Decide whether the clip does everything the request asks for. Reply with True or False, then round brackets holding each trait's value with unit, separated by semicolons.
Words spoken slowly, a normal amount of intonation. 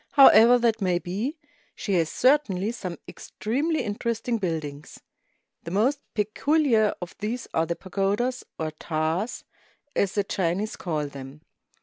False (130 wpm; 5.8 semitones)